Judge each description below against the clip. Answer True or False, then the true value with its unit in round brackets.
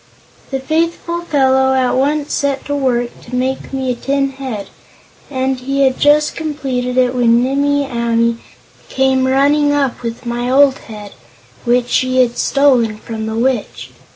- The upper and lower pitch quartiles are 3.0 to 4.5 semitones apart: False (2.4 semitones)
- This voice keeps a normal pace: True (155 wpm)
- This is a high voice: True (265 Hz)